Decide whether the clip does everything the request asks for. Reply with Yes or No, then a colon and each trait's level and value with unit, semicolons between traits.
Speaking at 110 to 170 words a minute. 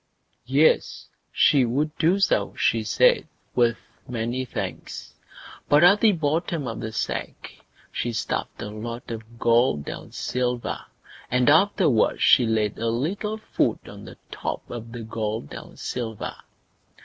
Yes: average, 140 wpm